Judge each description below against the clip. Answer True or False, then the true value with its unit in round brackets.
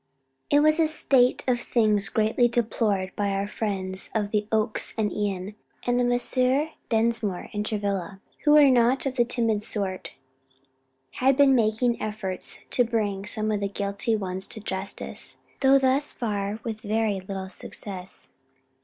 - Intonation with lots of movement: False (3.5 semitones)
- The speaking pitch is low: False (215 Hz)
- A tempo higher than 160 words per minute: False (155 wpm)